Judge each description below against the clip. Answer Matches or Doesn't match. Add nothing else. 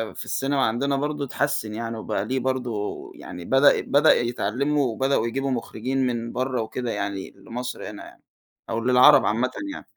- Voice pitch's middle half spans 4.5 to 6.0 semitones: Doesn't match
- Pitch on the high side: Doesn't match